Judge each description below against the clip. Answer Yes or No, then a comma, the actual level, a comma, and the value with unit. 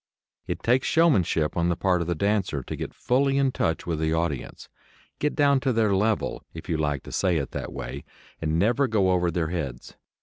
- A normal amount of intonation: No, wide, 6.9 semitones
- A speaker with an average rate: No, fast, 210 wpm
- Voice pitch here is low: Yes, very low, 90 Hz